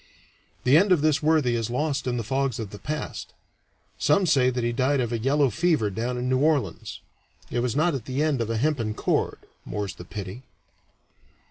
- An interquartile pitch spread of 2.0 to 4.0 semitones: No, average, 4.4 semitones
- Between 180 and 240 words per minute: Yes, fast, 205 wpm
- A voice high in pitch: No, low, 130 Hz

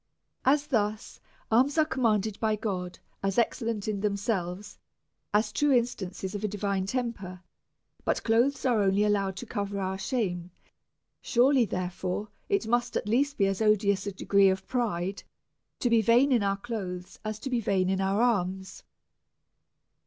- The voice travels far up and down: No, average, 3.6 semitones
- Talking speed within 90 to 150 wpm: No, average, 160 wpm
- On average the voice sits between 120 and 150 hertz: No, high, 210 Hz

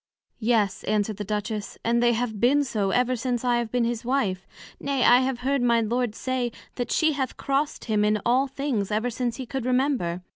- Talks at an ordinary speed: No, fast, 210 wpm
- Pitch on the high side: Yes, high, 240 Hz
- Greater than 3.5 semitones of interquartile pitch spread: No, average, 3.1 semitones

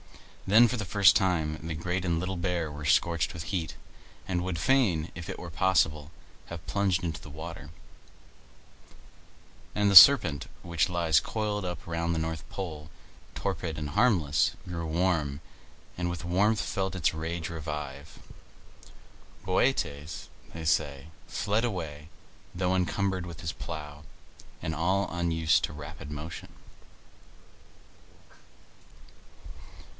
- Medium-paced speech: No, slow, 130 wpm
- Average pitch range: Yes, average, 3.0 semitones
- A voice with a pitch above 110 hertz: No, very low, 85 Hz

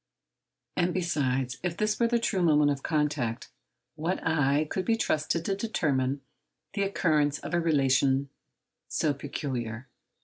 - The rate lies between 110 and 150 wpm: Yes, average, 140 wpm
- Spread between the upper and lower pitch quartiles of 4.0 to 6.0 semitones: Yes, average, 4.4 semitones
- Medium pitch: Yes, medium, 150 Hz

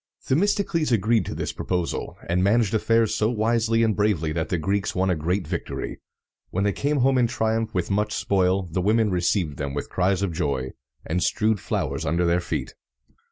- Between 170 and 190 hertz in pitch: No, low, 100 Hz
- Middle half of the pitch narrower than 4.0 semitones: No, average, 4.3 semitones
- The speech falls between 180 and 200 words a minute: Yes, average, 190 wpm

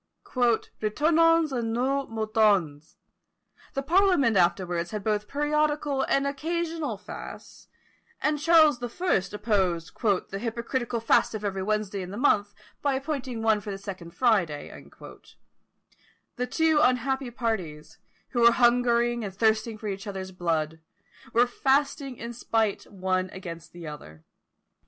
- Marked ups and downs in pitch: Yes, wide, 5.7 semitones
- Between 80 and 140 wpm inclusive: Yes, slow, 135 wpm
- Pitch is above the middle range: Yes, high, 225 Hz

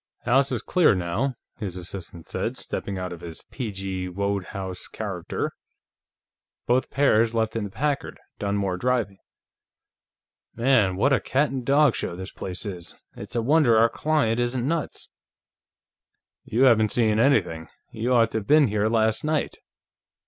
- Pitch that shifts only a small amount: No, average, 5.2 semitones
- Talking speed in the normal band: Yes, average, 155 wpm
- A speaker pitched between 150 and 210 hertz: No, low, 110 Hz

